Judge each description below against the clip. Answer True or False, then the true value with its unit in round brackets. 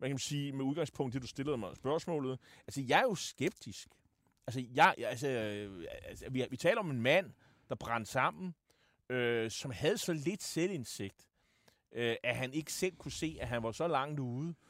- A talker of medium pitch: False (130 Hz)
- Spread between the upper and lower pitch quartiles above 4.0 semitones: True (4.4 semitones)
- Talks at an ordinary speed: True (190 wpm)